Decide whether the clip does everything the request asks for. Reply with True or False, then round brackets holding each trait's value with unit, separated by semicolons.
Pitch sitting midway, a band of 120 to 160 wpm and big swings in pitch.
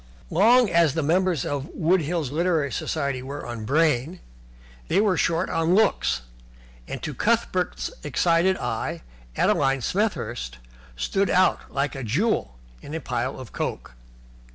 True (155 Hz; 140 wpm; 5.7 semitones)